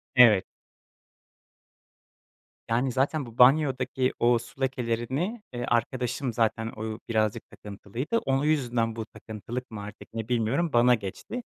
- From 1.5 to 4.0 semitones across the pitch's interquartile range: Yes, average, 2.9 semitones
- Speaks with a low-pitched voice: Yes, low, 120 Hz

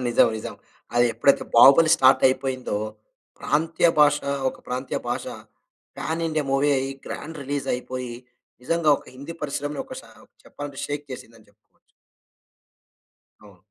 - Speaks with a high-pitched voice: No, low, 135 Hz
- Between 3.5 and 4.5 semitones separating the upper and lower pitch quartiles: No, average, 2.9 semitones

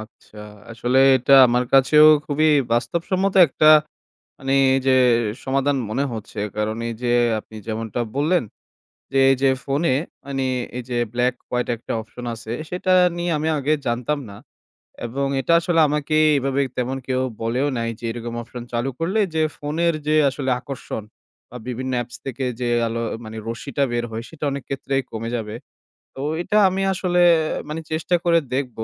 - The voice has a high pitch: No, low, 135 Hz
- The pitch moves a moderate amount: Yes, average, 4.2 semitones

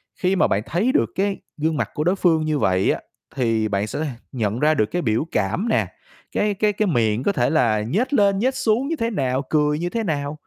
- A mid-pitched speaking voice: Yes, medium, 155 Hz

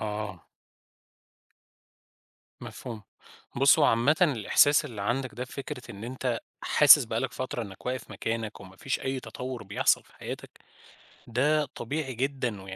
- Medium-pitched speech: No, low, 125 Hz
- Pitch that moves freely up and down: No, average, 3.7 semitones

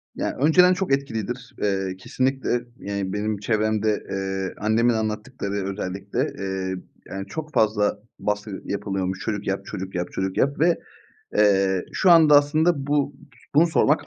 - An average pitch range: No, wide, 6.0 semitones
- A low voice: Yes, low, 105 Hz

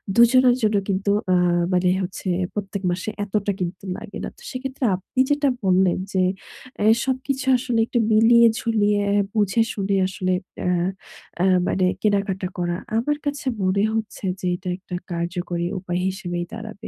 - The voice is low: No, high, 200 Hz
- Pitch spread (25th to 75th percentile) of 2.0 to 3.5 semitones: No, average, 3.9 semitones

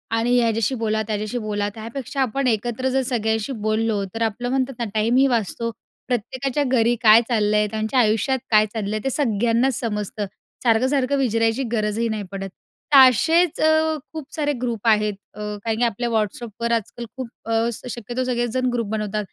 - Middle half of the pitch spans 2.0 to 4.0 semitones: Yes, average, 3.0 semitones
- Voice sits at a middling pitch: No, high, 230 Hz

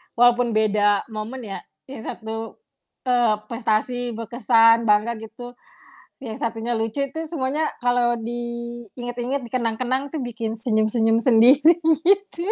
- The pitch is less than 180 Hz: No, high, 235 Hz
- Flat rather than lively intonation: Yes, narrow, 2.2 semitones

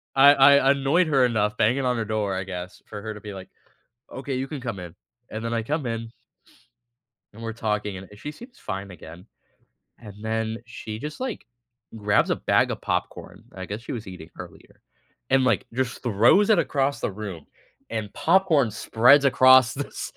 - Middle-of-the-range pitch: No, low, 115 Hz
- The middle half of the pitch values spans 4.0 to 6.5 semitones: Yes, average, 4.6 semitones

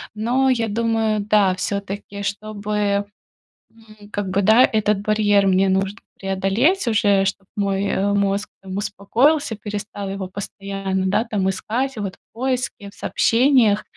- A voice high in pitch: Yes, high, 205 Hz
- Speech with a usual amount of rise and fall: No, narrow, 2.1 semitones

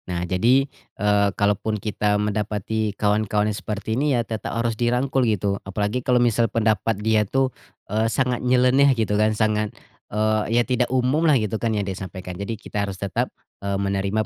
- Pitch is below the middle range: Yes, low, 110 Hz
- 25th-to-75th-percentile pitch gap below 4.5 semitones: Yes, average, 2.8 semitones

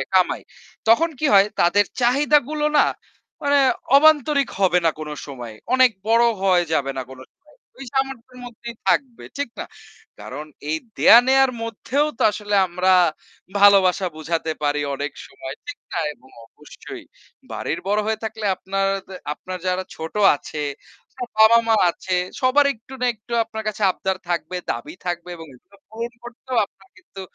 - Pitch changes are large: Yes, wide, 6.0 semitones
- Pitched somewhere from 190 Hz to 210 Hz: Yes, high, 205 Hz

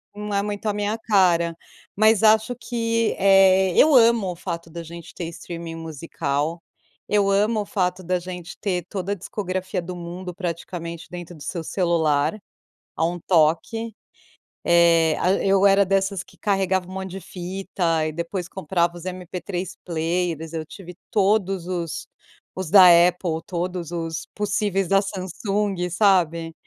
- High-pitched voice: No, medium, 180 Hz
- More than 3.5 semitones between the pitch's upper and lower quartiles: No, average, 2.7 semitones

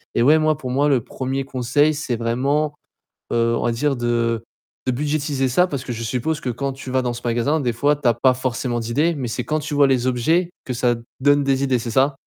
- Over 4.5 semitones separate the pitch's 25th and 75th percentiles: No, average, 3.3 semitones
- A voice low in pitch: Yes, low, 130 Hz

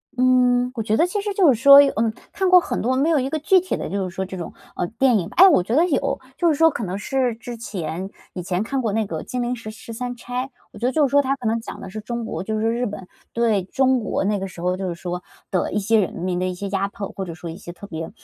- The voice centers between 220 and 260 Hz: Yes, high, 225 Hz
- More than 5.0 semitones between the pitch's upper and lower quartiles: Yes, wide, 5.5 semitones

